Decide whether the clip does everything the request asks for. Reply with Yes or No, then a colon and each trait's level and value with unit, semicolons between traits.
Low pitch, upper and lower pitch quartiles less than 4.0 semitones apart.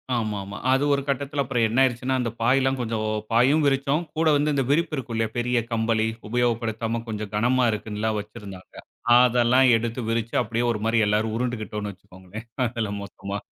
Yes: low, 115 Hz; average, 2.9 semitones